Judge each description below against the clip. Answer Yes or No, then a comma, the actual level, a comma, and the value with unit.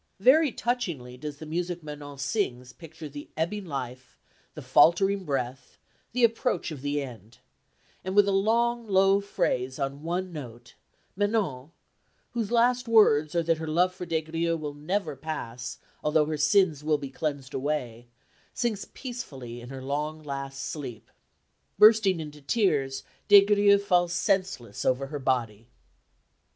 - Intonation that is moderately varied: No, wide, 6.3 semitones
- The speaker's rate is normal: Yes, average, 150 wpm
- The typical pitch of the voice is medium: Yes, medium, 155 Hz